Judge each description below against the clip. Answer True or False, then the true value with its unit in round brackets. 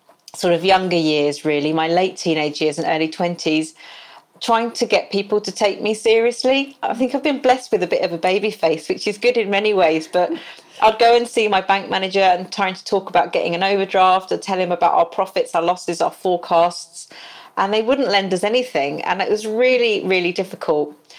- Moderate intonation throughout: True (4.1 semitones)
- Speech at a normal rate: False (215 wpm)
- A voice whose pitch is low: False (190 Hz)